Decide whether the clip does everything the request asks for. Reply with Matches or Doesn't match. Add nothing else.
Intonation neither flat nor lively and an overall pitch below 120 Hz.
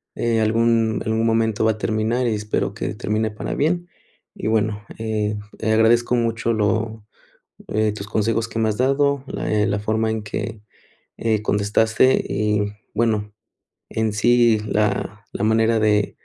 Doesn't match